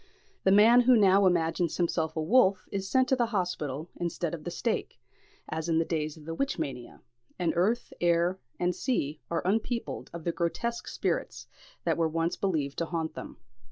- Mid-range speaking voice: Yes, medium, 175 Hz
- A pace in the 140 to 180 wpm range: No, average, 190 wpm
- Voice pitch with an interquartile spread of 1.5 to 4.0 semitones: Yes, average, 3.7 semitones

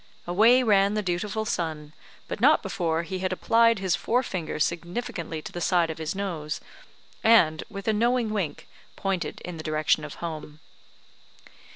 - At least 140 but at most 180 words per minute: Yes, average, 160 wpm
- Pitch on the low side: No, medium, 185 Hz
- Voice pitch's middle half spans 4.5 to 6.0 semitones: Yes, average, 4.9 semitones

